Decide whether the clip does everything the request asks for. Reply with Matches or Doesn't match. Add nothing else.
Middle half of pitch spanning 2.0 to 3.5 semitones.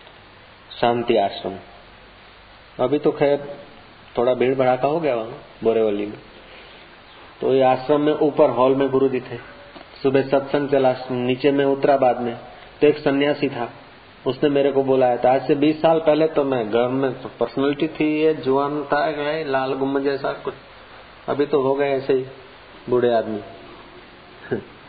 Matches